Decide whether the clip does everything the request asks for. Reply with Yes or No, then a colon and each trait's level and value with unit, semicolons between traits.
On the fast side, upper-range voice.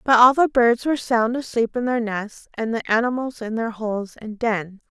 Yes: fast, 215 wpm; high, 230 Hz